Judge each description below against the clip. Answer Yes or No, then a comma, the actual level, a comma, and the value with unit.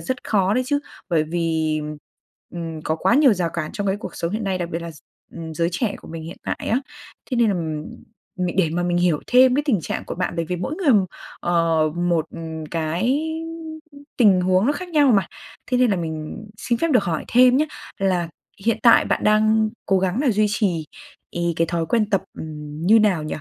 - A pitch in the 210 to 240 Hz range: No, medium, 185 Hz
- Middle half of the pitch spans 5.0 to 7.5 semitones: Yes, average, 5.3 semitones